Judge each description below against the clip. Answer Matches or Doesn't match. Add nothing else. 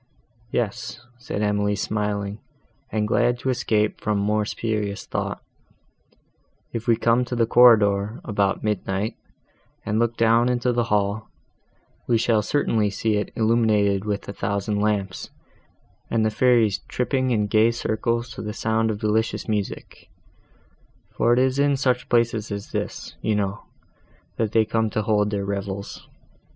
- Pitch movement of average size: Doesn't match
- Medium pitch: Doesn't match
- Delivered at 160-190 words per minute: Doesn't match